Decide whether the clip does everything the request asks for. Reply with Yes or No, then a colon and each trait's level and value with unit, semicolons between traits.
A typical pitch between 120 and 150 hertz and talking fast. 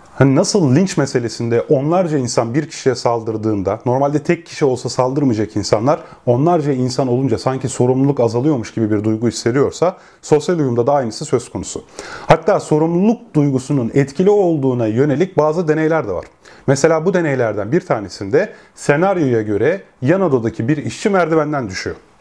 Yes: medium, 140 Hz; fast, 145 wpm